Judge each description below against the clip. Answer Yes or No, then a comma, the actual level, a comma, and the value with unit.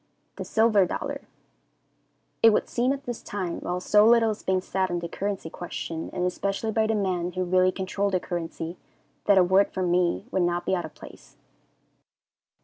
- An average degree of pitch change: Yes, average, 3.0 semitones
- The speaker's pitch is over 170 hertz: Yes, high, 190 Hz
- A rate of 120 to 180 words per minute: No, average, 190 wpm